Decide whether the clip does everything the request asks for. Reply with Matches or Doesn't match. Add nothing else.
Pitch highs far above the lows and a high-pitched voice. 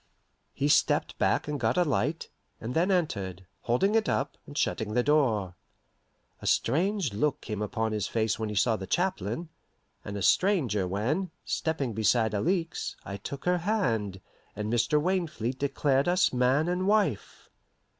Doesn't match